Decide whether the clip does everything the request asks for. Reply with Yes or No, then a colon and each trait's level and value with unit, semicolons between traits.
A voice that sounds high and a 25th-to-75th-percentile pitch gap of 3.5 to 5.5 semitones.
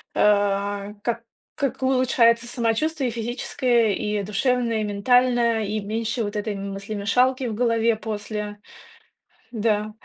No: high, 225 Hz; narrow, 2.6 semitones